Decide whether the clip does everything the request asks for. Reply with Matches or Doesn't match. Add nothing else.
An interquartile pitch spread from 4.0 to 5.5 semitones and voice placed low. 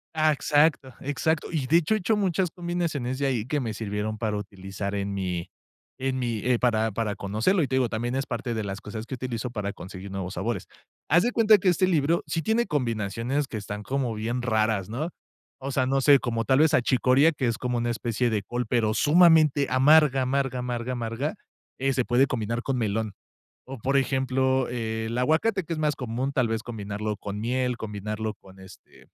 Matches